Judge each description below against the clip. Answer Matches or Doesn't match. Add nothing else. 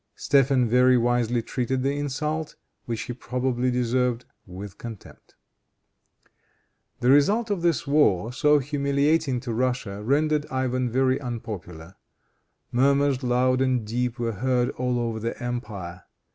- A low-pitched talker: Matches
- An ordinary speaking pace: Doesn't match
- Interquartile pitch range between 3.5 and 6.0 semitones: Doesn't match